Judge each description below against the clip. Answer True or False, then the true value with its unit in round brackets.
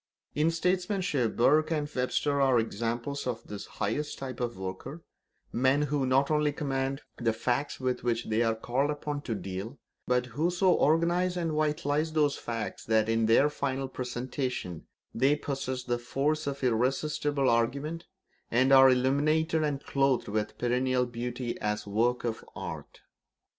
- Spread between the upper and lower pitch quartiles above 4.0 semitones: False (3.7 semitones)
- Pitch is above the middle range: False (135 Hz)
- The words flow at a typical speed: True (155 wpm)